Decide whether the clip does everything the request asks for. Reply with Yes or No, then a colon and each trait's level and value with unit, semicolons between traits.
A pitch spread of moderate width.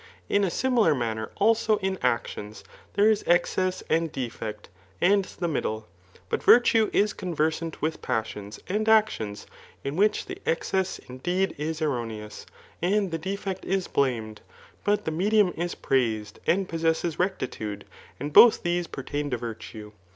No: wide, 8.2 semitones